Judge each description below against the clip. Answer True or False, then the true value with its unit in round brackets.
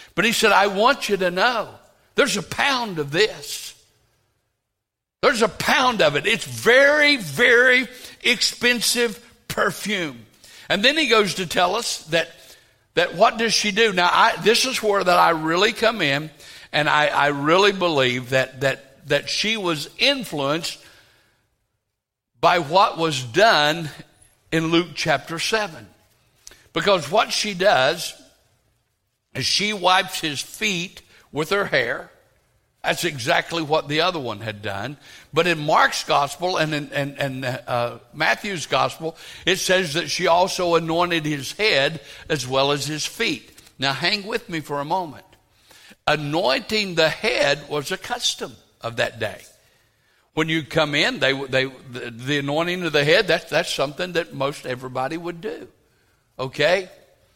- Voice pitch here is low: False (160 Hz)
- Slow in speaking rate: False (155 wpm)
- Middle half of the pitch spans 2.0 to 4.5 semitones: False (5.6 semitones)